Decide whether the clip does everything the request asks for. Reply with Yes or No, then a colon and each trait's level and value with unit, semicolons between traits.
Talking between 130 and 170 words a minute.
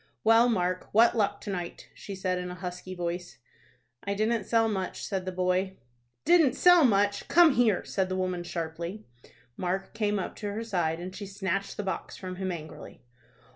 No: average, 185 wpm